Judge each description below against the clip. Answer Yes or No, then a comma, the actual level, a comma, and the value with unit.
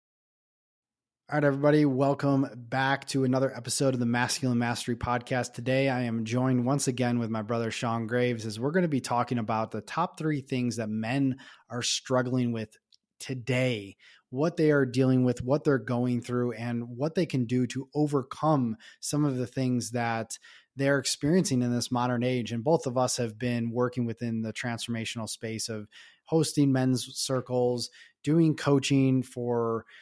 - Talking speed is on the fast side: No, average, 170 wpm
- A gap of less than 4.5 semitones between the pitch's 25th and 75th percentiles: Yes, narrow, 2.4 semitones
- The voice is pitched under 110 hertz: No, low, 125 Hz